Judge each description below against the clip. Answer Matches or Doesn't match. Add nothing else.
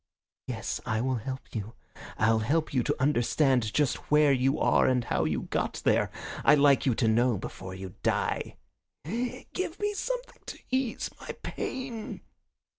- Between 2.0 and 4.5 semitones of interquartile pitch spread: Doesn't match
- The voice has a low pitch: Matches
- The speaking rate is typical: Matches